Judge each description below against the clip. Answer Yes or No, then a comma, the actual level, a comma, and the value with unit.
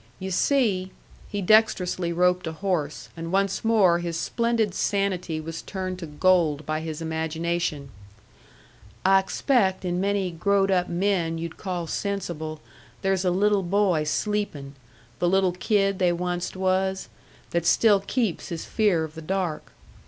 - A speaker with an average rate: Yes, average, 145 wpm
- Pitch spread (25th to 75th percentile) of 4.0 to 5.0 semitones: No, average, 3.0 semitones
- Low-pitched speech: No, medium, 180 Hz